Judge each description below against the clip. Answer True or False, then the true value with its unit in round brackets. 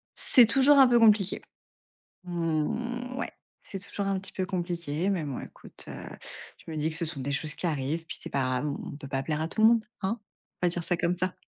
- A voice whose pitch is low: False (175 Hz)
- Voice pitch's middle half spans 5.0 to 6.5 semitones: True (5.4 semitones)